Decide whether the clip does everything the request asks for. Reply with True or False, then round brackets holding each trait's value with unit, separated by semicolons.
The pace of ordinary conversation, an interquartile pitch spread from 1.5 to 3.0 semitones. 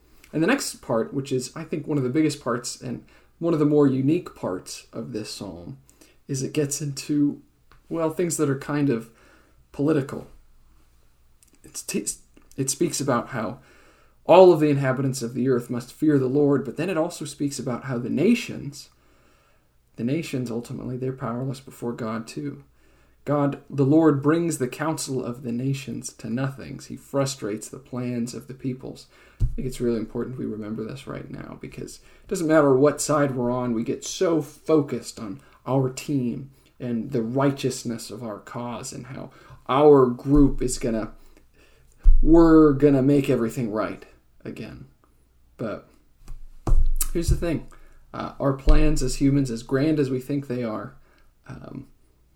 False (165 wpm; 3.6 semitones)